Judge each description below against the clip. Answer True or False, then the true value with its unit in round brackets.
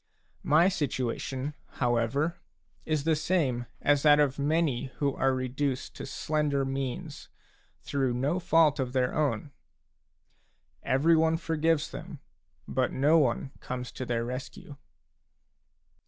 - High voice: False (140 Hz)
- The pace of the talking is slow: True (125 wpm)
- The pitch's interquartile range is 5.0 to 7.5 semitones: False (3.3 semitones)